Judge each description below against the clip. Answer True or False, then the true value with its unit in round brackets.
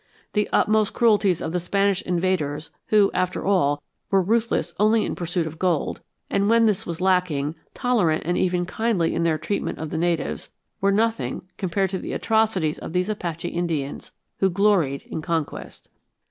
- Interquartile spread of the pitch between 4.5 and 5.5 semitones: False (3.8 semitones)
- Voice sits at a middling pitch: True (180 Hz)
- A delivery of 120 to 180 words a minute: True (170 wpm)